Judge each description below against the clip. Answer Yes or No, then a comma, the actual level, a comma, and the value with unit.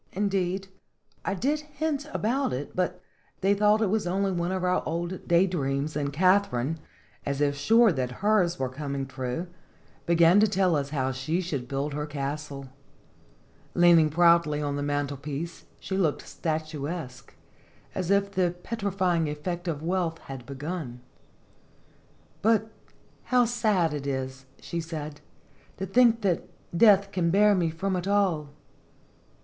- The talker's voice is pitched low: No, medium, 170 Hz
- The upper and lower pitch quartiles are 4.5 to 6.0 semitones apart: Yes, average, 5.1 semitones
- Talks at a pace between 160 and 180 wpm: No, average, 145 wpm